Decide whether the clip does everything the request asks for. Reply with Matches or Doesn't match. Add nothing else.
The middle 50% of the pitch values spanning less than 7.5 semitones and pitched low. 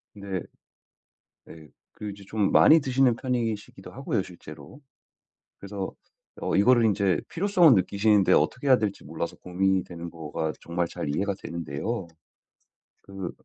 Matches